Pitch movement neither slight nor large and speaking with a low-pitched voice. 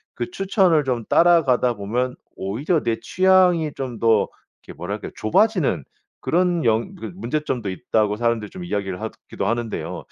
No: wide, 8.1 semitones; low, 125 Hz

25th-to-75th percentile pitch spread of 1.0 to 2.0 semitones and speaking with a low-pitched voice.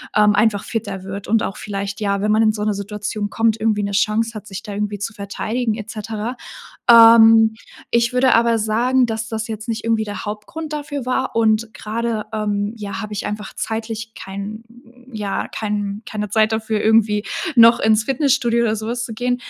No: narrow, 1.7 semitones; high, 220 Hz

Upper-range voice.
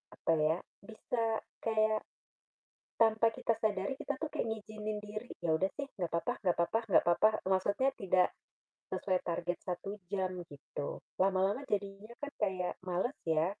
Yes: high, 200 Hz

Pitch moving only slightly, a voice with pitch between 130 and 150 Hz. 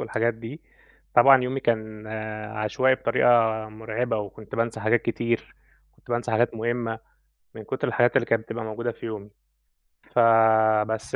No: narrow, 1.5 semitones; low, 115 Hz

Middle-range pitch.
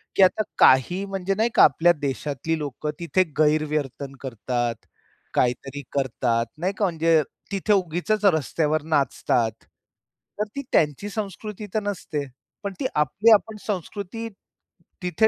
Yes: medium, 165 Hz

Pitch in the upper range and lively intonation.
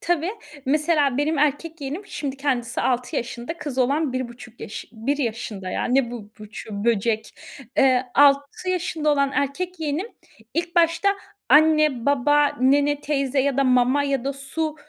No: very high, 280 Hz; average, 3.4 semitones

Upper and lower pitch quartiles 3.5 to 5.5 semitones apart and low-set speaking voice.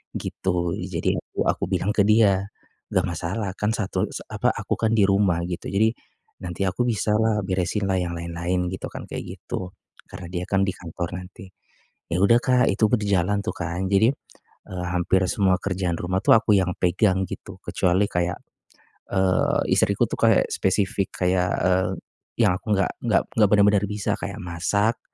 No: narrow, 2.4 semitones; very low, 95 Hz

